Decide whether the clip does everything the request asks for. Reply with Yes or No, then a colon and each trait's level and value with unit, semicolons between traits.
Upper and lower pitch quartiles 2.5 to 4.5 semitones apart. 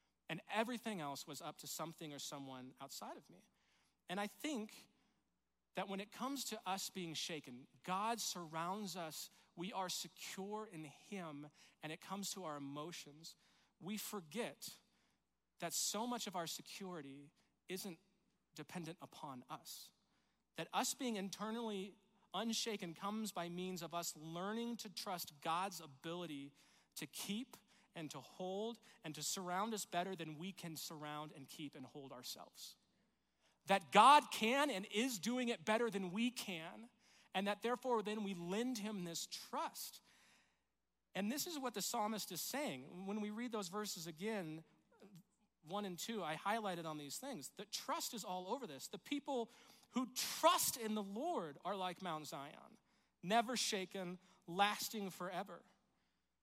No: average, 5.0 semitones